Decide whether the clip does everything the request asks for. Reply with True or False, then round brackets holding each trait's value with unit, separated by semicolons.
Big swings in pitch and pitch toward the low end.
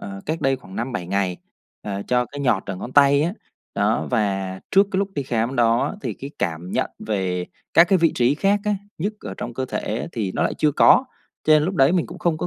True (8.0 semitones; 125 Hz)